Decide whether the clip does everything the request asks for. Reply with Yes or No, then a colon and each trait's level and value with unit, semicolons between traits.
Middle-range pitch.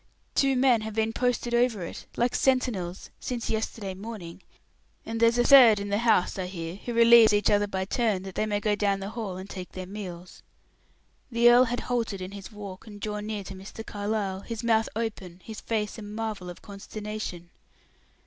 No: high, 210 Hz